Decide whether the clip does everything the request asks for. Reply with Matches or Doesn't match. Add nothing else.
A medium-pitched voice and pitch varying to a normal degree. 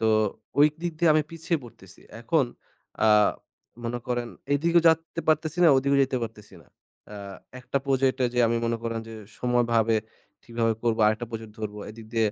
Doesn't match